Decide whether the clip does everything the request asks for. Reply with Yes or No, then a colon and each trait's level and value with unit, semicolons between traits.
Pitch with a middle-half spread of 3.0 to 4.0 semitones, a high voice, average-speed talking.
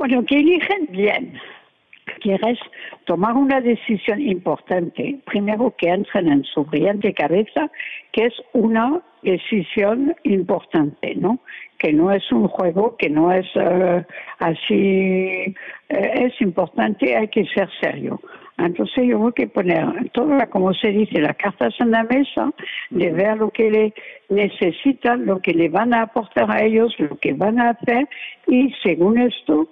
No: average, 5.0 semitones; high, 215 Hz; average, 150 wpm